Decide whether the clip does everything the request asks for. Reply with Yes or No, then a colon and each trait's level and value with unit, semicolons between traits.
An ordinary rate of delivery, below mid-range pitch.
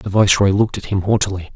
No: fast, 230 wpm; low, 100 Hz